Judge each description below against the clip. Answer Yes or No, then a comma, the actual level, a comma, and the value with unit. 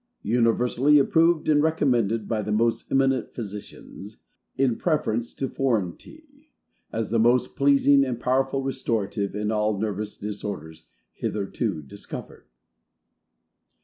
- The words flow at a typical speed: No, slow, 115 wpm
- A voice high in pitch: No, low, 115 Hz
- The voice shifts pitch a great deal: No, average, 4.4 semitones